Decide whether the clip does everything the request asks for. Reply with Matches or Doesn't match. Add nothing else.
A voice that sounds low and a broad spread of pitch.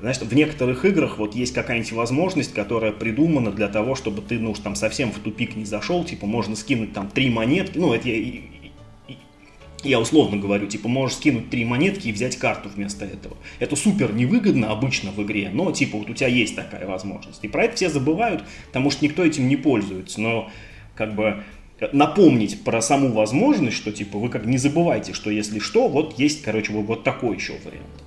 Doesn't match